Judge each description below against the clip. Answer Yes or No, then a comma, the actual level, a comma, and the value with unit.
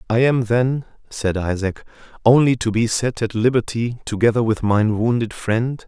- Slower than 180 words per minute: Yes, average, 165 wpm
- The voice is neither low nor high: No, low, 115 Hz